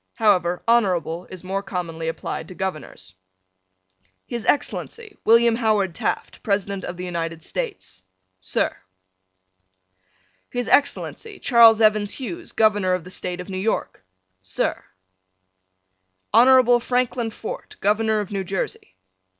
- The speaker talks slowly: Yes, slow, 120 wpm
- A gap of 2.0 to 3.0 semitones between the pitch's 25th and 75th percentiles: No, average, 4.5 semitones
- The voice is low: No, high, 205 Hz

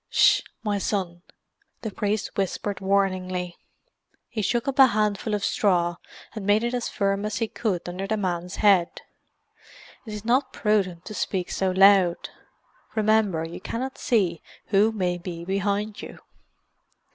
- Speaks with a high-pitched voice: Yes, high, 200 Hz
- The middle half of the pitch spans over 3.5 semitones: No, average, 2.8 semitones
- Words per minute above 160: No, average, 155 wpm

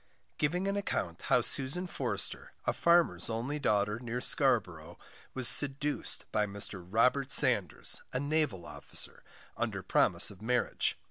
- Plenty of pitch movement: Yes, wide, 6.0 semitones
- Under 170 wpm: Yes, slow, 135 wpm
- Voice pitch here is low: Yes, low, 125 Hz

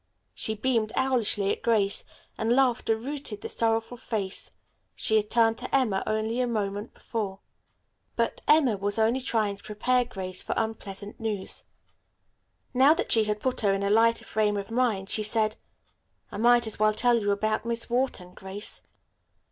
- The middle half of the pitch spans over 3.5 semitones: No, narrow, 2.6 semitones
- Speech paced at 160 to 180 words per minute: Yes, average, 170 wpm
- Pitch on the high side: Yes, high, 220 Hz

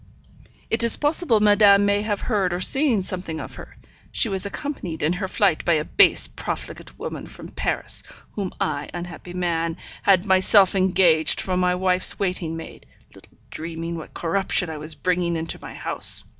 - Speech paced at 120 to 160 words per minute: No, average, 170 wpm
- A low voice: No, medium, 185 Hz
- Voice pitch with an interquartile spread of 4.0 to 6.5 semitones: No, average, 3.3 semitones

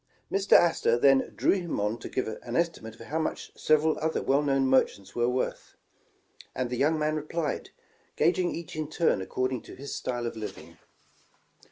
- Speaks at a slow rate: No, average, 185 wpm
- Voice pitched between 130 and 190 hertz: Yes, medium, 140 Hz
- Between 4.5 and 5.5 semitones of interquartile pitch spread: Yes, average, 4.8 semitones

